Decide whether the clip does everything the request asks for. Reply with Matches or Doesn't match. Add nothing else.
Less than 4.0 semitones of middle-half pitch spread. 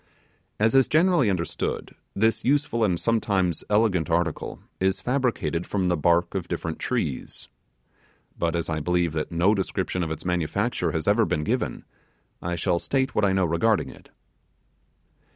Doesn't match